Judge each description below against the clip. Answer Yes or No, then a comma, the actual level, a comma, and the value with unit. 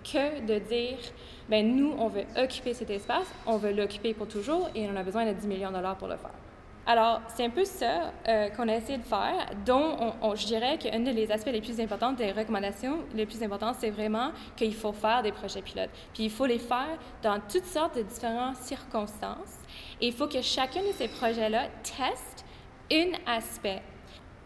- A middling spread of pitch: Yes, average, 3.0 semitones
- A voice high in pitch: Yes, high, 230 Hz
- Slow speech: No, average, 205 wpm